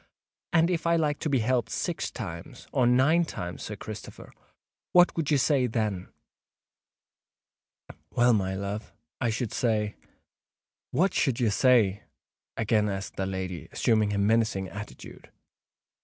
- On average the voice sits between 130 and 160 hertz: No, low, 115 Hz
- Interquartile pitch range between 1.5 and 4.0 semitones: No, average, 4.6 semitones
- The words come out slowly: Yes, slow, 125 wpm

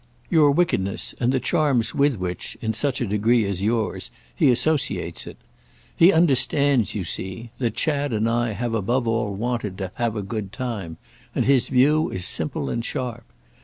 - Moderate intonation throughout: Yes, average, 4.4 semitones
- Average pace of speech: Yes, average, 175 wpm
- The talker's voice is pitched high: No, low, 120 Hz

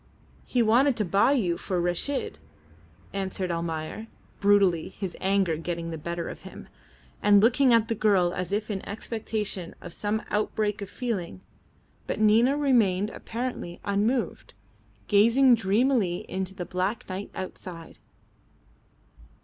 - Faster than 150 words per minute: No, slow, 135 wpm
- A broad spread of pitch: No, average, 4.1 semitones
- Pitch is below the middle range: No, high, 200 Hz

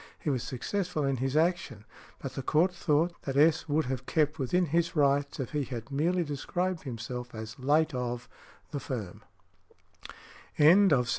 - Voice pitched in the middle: Yes, medium, 145 Hz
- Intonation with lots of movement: No, average, 4.2 semitones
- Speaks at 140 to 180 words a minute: Yes, average, 155 wpm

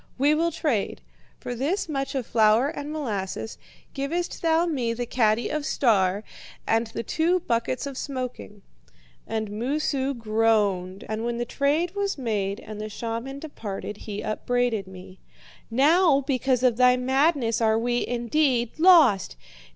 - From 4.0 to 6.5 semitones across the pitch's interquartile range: Yes, average, 4.5 semitones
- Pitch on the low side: No, high, 245 Hz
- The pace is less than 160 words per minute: Yes, average, 145 wpm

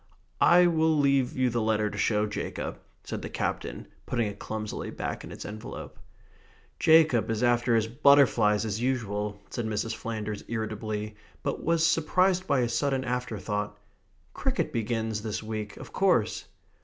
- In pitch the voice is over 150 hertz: No, low, 115 Hz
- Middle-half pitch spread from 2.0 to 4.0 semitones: Yes, average, 3.6 semitones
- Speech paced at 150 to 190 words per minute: Yes, average, 155 wpm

